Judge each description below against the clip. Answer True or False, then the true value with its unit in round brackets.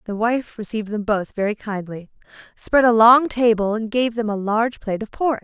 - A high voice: True (220 Hz)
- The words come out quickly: True (210 wpm)